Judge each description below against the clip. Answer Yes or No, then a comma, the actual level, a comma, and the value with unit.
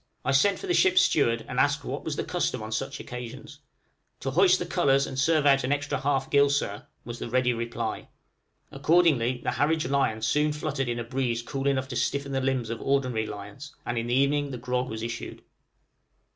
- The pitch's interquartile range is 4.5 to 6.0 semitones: No, average, 3.2 semitones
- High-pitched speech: No, low, 135 Hz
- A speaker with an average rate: No, fast, 210 wpm